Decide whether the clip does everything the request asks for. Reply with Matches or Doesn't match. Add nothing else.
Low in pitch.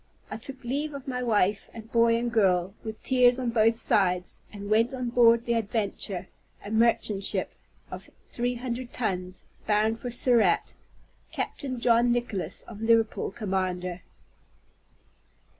Doesn't match